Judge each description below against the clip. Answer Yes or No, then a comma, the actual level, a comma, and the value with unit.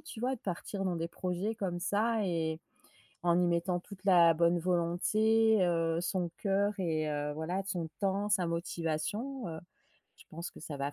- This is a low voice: No, medium, 175 Hz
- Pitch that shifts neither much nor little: Yes, average, 3.2 semitones